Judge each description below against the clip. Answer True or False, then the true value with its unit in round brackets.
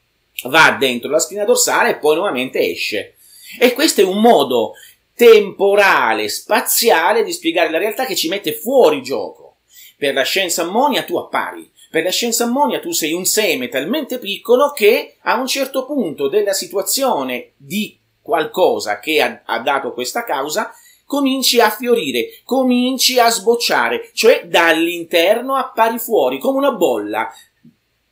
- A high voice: True (245 Hz)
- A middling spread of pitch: False (6.5 semitones)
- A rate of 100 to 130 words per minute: False (145 wpm)